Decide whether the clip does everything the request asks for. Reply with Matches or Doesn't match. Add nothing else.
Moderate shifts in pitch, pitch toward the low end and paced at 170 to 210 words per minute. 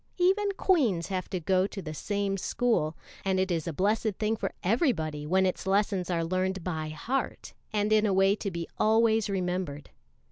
Doesn't match